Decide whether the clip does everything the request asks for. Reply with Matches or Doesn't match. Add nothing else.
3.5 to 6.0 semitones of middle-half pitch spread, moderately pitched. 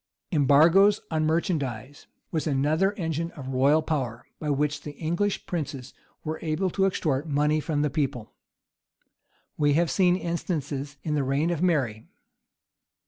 Doesn't match